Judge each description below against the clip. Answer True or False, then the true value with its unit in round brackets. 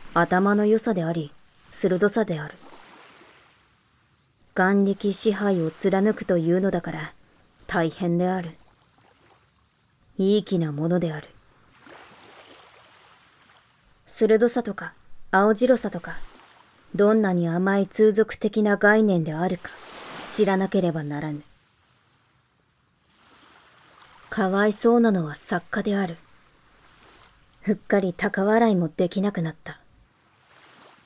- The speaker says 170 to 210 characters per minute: True (195 characters per minute)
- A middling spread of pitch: True (3.5 semitones)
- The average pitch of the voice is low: False (190 Hz)